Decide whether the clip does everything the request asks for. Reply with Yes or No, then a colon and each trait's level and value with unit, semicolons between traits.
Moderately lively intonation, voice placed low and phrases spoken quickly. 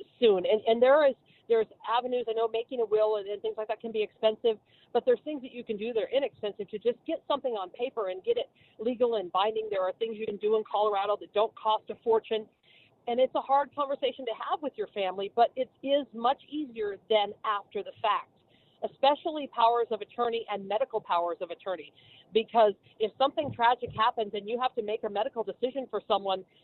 No: average, 3.3 semitones; high, 225 Hz; fast, 220 wpm